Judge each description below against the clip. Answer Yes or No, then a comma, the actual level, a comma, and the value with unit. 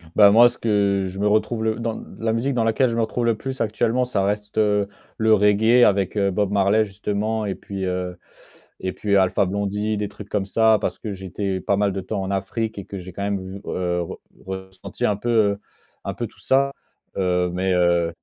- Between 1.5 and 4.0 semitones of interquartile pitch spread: Yes, narrow, 2.5 semitones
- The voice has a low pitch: Yes, low, 100 Hz